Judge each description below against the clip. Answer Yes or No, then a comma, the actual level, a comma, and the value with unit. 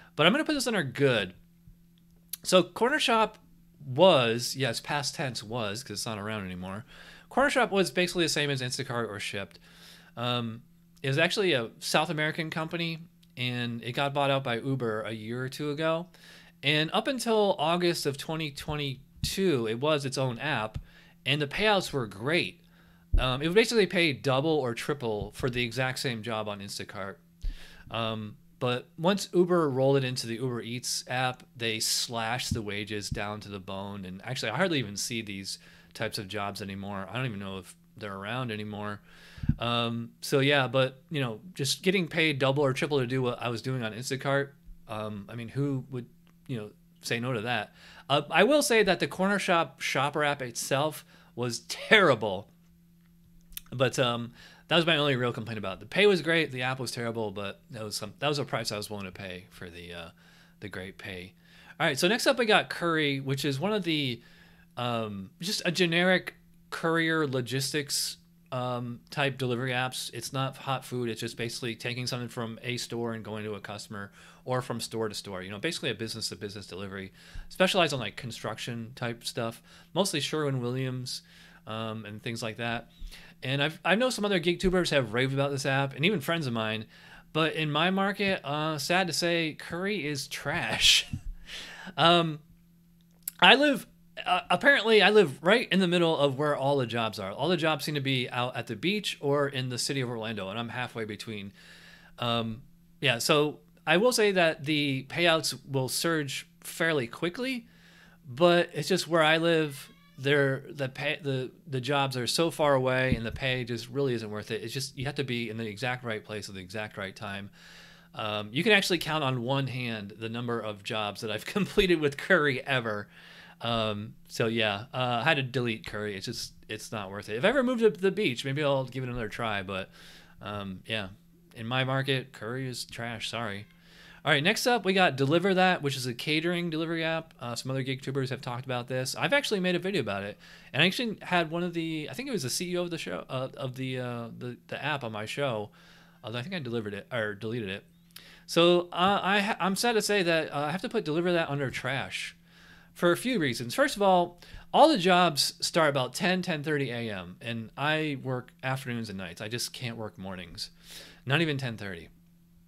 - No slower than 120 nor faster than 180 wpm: No, fast, 205 wpm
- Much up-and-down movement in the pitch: Yes, wide, 6.6 semitones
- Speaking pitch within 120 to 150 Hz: Yes, low, 135 Hz